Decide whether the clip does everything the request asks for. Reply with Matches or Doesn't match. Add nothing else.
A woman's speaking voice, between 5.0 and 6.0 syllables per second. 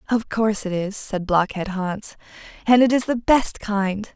Doesn't match